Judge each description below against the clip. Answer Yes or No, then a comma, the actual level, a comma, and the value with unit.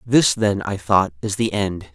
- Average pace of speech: No, fast, 215 wpm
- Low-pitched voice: Yes, low, 100 Hz